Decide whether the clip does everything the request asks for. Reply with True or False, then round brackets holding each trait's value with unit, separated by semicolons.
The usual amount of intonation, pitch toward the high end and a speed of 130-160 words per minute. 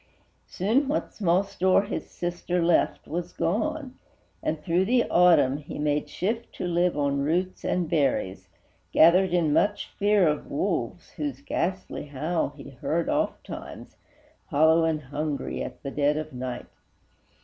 False (4.1 semitones; 170 Hz; 145 wpm)